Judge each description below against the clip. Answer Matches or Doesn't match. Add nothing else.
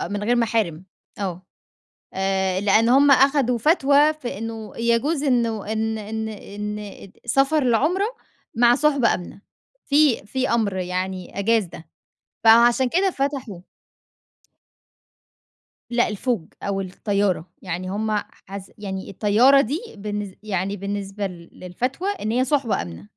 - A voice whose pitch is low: Doesn't match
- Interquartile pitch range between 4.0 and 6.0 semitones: Matches